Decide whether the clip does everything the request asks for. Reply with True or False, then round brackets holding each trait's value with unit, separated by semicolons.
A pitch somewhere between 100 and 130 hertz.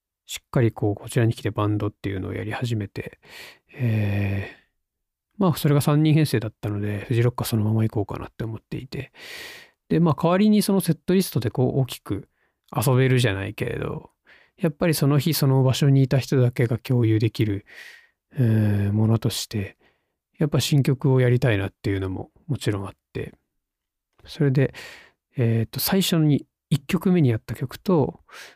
True (125 Hz)